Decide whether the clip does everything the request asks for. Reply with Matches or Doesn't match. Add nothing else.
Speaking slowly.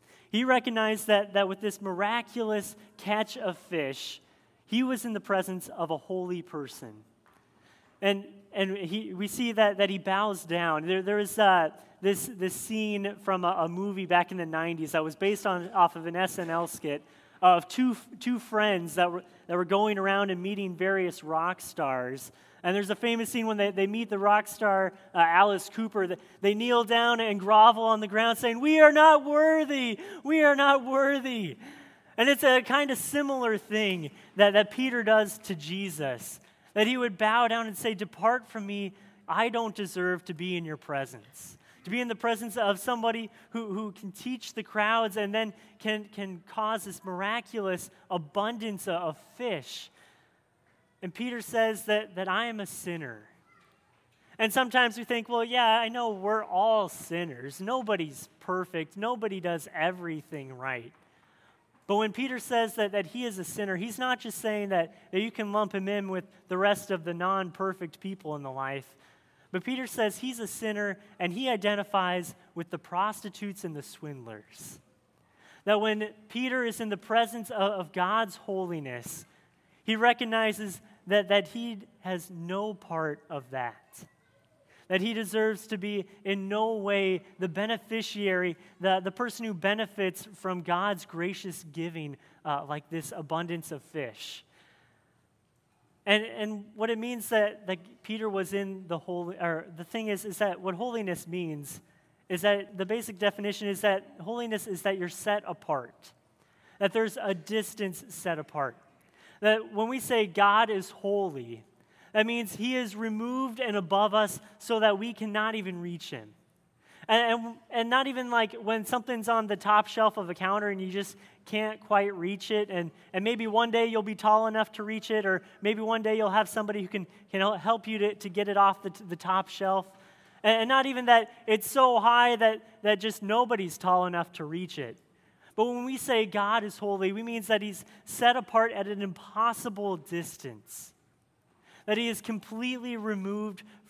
Doesn't match